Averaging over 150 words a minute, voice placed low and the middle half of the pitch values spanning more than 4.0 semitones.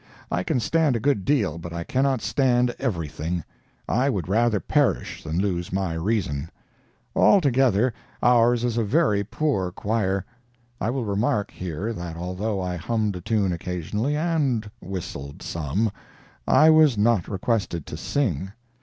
No: average, 145 wpm; low, 105 Hz; wide, 5.4 semitones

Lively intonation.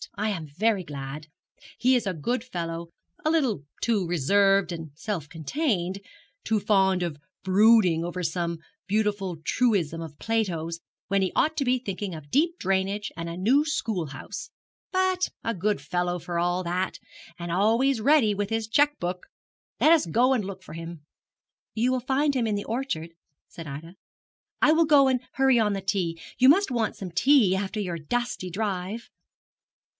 Yes: wide, 5.9 semitones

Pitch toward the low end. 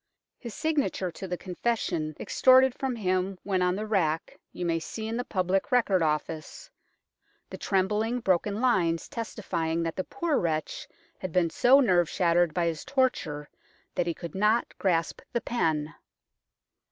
No: medium, 185 Hz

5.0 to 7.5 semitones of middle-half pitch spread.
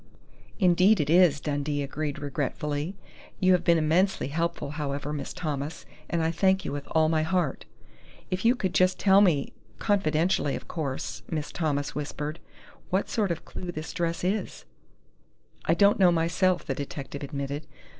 No: average, 4.0 semitones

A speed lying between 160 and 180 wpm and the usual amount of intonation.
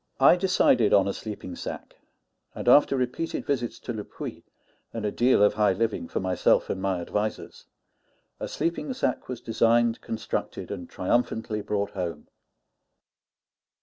No: average, 150 wpm; average, 3.7 semitones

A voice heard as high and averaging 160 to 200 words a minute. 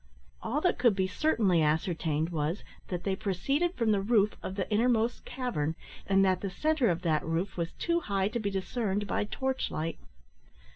Yes: high, 195 Hz; average, 185 wpm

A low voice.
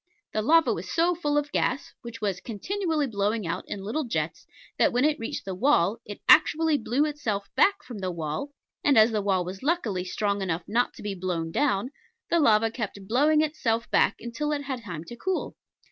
No: high, 230 Hz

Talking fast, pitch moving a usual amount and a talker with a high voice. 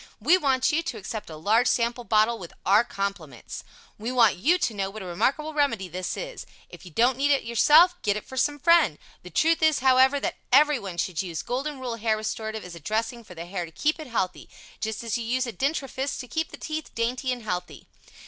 No: fast, 225 wpm; wide, 5.8 semitones; high, 235 Hz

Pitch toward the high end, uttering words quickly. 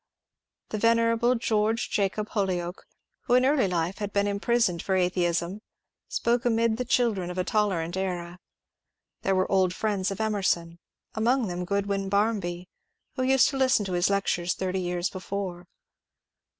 No: high, 200 Hz; average, 150 wpm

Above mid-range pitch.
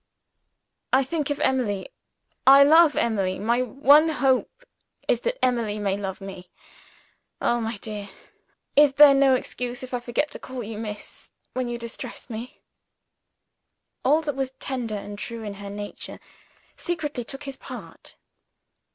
Yes: very high, 250 Hz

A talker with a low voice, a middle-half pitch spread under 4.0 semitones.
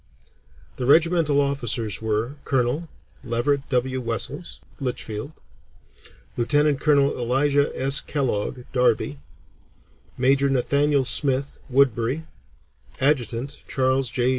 Yes: low, 130 Hz; average, 2.7 semitones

